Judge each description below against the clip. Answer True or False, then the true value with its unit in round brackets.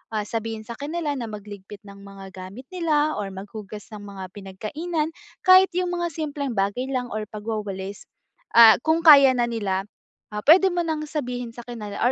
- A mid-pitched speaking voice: False (230 Hz)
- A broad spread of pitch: True (6.9 semitones)